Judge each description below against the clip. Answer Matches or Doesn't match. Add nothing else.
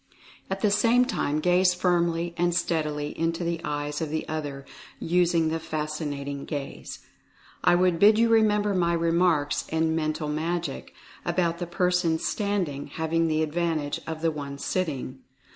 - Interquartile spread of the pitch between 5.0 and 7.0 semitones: Doesn't match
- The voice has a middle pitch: Matches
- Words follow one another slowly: Doesn't match